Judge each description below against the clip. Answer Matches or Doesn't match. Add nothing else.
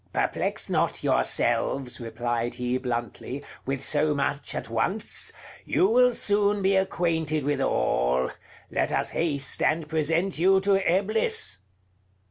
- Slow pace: Matches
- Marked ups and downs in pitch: Matches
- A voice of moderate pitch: Matches